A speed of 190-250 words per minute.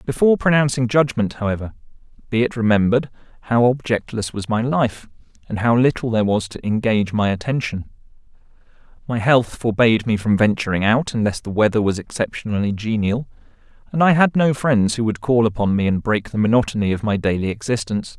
No: average, 170 wpm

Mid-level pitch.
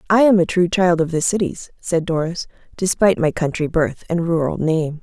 Yes: medium, 170 Hz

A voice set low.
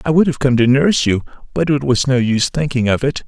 Yes: low, 130 Hz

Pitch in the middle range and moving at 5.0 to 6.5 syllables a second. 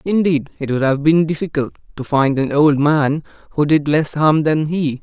No: medium, 150 Hz; 4.7 syllables/s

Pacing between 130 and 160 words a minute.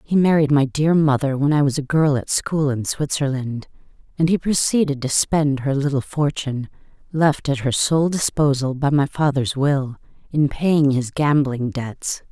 No: average, 175 wpm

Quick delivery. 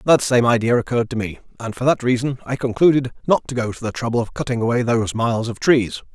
Yes: fast, 245 wpm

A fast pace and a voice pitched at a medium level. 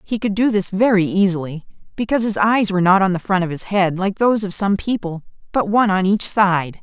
No: fast, 235 wpm; high, 195 Hz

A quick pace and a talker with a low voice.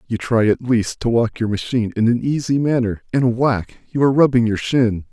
Yes: fast, 210 wpm; low, 120 Hz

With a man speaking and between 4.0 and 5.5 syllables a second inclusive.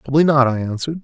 No: male; 8.6 syllables/s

